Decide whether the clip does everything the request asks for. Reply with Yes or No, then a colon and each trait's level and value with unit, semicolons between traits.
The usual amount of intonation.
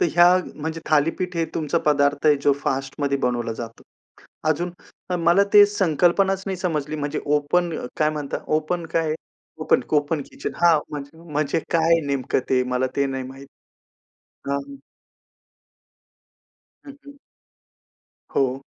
Yes: average, 3.4 semitones